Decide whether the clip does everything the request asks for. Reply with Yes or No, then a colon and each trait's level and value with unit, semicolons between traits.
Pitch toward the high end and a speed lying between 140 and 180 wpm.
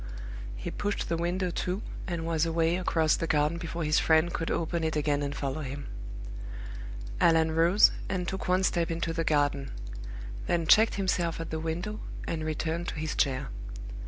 No: medium, 165 Hz; average, 175 wpm